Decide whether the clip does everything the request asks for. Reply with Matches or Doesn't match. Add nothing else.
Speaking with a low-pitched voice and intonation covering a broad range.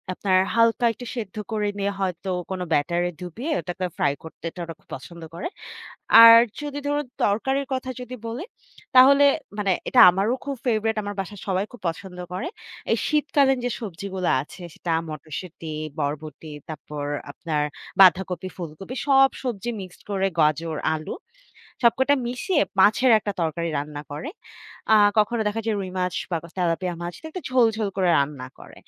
Doesn't match